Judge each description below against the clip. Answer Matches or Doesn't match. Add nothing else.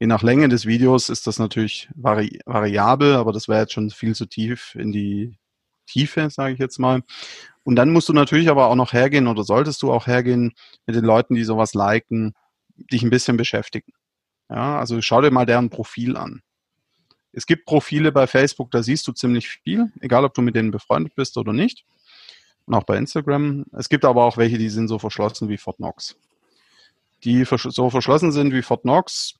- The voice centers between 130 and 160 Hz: Doesn't match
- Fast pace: Matches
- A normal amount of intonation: Matches